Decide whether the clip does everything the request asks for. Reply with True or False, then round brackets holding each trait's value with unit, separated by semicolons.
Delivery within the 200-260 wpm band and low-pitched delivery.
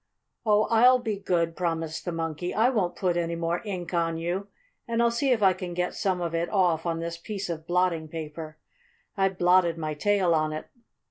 False (205 wpm; 175 Hz)